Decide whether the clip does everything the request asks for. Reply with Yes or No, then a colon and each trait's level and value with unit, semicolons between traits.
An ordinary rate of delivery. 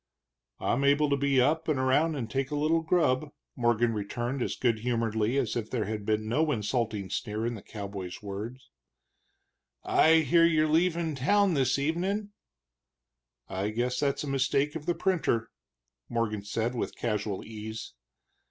Yes: average, 160 wpm